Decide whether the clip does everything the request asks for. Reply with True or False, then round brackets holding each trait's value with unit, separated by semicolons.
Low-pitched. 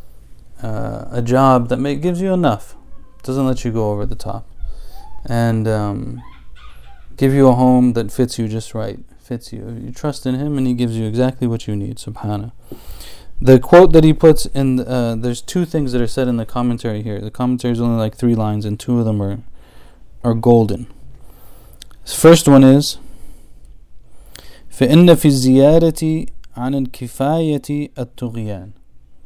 True (120 Hz)